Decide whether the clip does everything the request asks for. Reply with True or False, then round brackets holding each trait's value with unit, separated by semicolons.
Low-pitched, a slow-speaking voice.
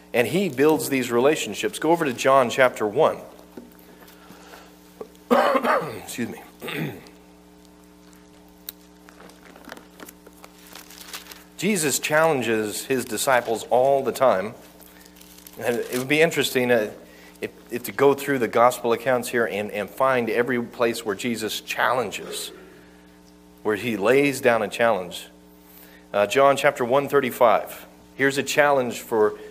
True (105 Hz; 115 wpm)